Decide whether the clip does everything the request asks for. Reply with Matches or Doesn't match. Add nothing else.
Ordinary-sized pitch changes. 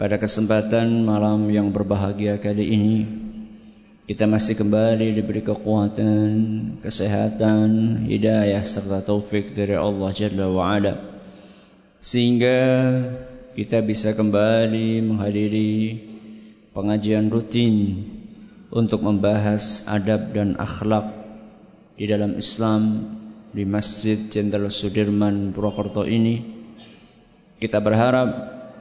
Doesn't match